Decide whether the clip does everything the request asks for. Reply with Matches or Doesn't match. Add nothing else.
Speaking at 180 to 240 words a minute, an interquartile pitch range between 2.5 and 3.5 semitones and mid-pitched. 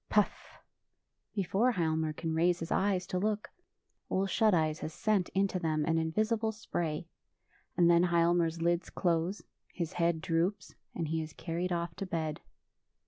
Doesn't match